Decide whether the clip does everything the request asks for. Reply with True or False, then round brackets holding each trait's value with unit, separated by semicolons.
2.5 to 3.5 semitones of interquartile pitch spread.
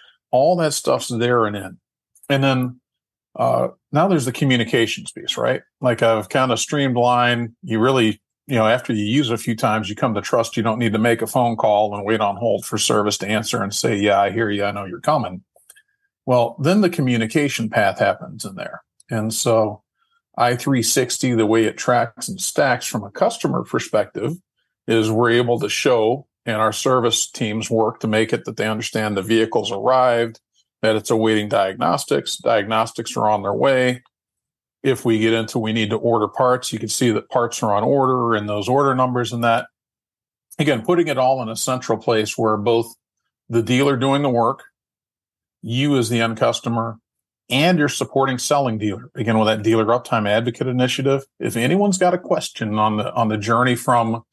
True (2.9 semitones)